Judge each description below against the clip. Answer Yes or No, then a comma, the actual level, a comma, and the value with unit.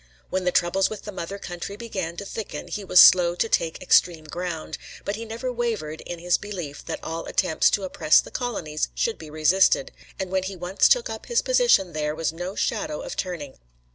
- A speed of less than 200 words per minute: No, fast, 205 wpm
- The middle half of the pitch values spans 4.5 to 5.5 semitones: No, average, 4.0 semitones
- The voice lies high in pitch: No, medium, 180 Hz